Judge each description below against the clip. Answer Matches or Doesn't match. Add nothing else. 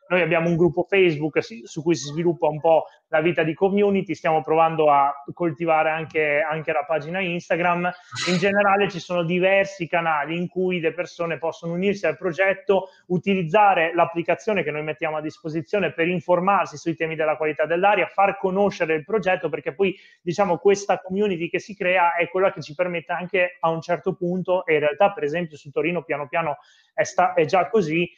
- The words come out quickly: Matches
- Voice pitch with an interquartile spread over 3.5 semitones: Doesn't match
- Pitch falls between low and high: Matches